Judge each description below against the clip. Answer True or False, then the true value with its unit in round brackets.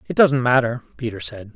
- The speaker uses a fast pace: False (195 wpm)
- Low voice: True (125 Hz)